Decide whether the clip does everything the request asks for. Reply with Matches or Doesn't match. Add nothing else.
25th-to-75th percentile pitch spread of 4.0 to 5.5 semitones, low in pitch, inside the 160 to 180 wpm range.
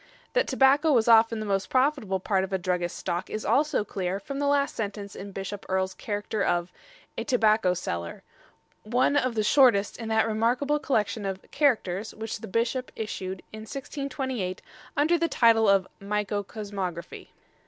Doesn't match